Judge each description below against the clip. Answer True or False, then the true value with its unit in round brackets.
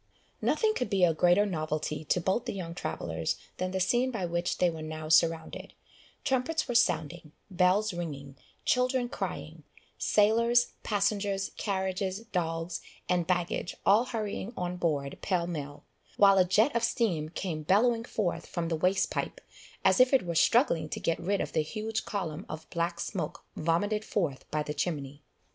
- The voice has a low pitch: False (180 Hz)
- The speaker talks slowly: False (165 wpm)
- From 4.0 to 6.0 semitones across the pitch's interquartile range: True (4.4 semitones)